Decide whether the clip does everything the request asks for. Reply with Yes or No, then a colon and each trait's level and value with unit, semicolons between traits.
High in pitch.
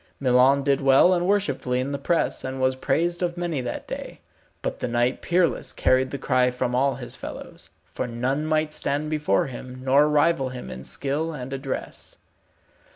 No: low, 135 Hz